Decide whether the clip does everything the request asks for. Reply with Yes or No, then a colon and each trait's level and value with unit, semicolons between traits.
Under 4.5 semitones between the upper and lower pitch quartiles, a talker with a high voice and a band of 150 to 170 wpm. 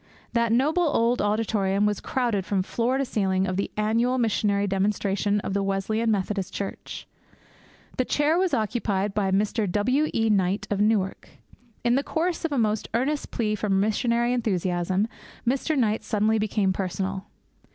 Yes: average, 3.4 semitones; high, 215 Hz; average, 160 wpm